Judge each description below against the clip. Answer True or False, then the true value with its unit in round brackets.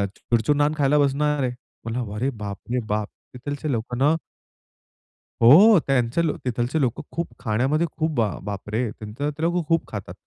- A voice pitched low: True (130 Hz)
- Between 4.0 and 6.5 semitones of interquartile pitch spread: True (4.5 semitones)